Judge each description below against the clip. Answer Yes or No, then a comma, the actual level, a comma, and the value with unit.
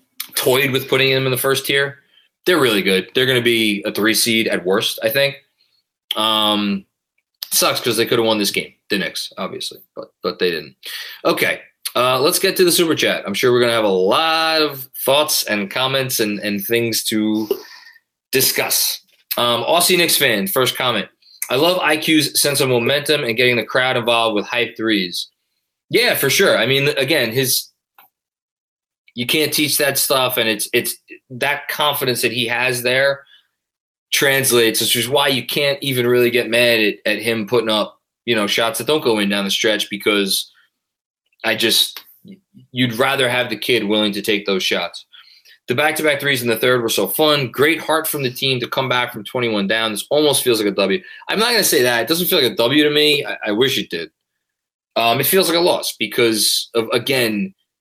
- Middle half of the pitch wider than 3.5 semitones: Yes, average, 4.6 semitones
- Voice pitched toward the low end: Yes, low, 125 Hz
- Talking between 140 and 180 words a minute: No, average, 200 wpm